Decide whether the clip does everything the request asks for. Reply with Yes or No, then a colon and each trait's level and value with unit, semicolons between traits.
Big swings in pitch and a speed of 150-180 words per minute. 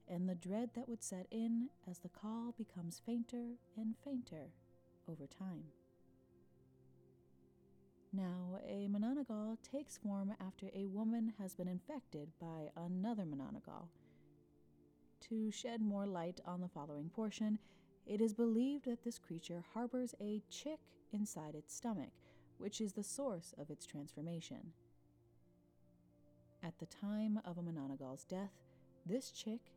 No: wide, 7.4 semitones; slow, 135 wpm